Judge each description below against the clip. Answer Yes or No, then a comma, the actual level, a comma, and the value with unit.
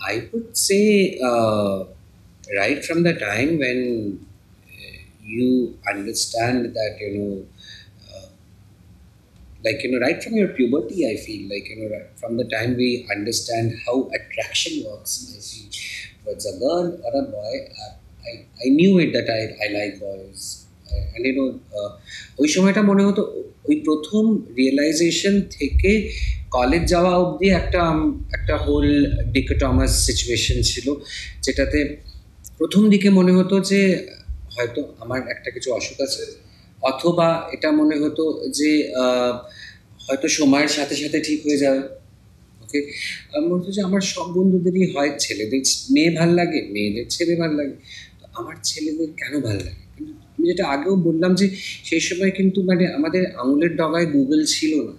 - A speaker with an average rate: No, fast, 145 wpm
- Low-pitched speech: No, medium, 145 Hz